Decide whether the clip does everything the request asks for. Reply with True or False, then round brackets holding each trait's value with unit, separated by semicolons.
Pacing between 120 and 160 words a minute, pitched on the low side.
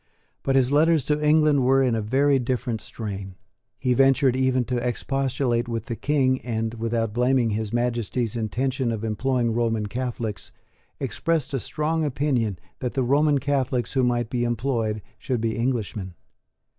True (155 wpm; 125 Hz)